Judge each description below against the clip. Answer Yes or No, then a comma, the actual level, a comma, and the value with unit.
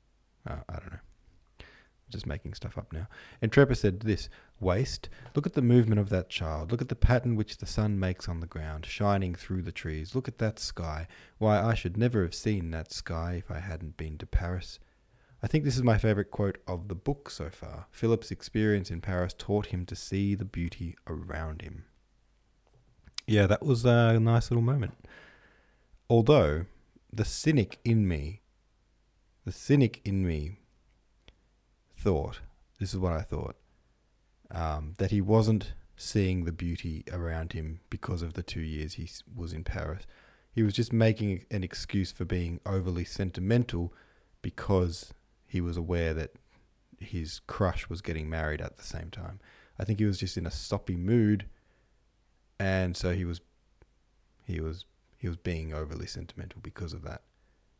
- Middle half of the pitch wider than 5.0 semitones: No, average, 4.1 semitones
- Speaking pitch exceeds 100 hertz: No, very low, 95 Hz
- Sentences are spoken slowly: No, average, 170 wpm